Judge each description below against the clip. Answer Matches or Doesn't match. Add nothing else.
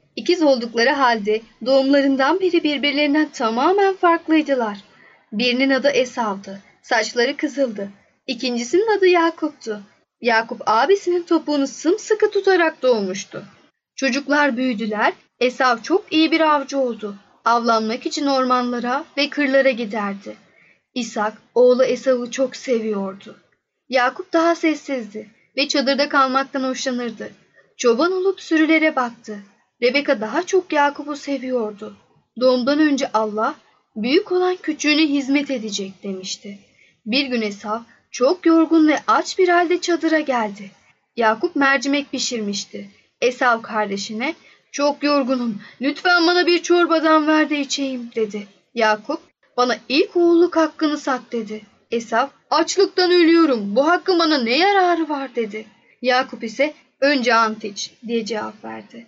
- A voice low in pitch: Doesn't match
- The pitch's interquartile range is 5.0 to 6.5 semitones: Matches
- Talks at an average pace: Matches